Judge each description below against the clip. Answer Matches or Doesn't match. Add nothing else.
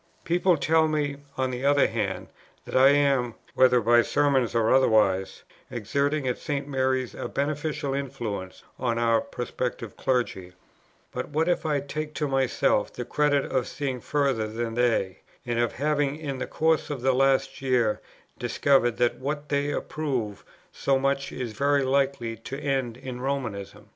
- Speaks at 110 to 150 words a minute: Doesn't match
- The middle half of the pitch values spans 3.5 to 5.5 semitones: Doesn't match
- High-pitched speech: Doesn't match